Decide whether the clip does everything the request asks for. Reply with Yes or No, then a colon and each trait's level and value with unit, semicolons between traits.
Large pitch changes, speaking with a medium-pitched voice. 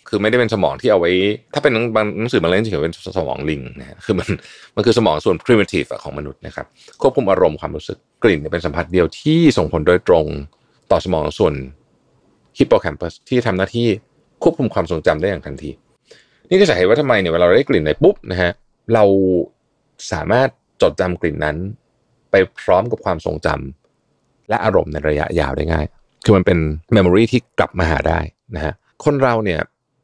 No: wide, 7.1 semitones; very low, 90 Hz